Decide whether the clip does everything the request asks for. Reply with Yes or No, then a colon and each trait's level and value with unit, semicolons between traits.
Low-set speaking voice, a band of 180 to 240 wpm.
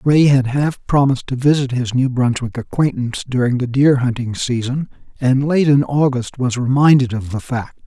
Yes: low, 130 Hz; average, 185 wpm